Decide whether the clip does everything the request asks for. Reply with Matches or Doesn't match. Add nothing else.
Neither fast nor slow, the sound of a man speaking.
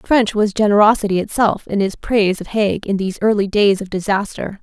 Doesn't match